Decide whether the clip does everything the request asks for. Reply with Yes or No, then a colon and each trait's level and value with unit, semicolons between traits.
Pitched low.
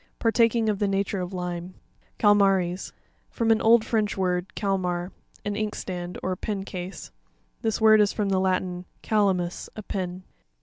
No: high, 195 Hz